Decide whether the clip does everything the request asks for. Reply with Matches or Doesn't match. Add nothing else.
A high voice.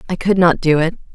Doesn't match